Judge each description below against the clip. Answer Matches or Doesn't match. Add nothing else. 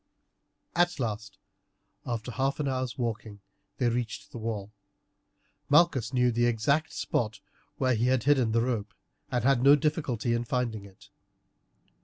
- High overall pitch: Doesn't match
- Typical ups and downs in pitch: Matches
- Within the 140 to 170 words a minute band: Matches